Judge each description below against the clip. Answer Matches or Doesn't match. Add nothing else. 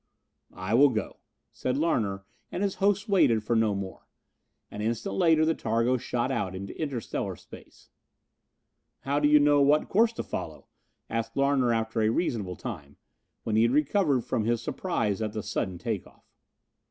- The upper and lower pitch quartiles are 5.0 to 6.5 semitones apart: Matches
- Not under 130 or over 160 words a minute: Doesn't match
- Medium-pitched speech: Doesn't match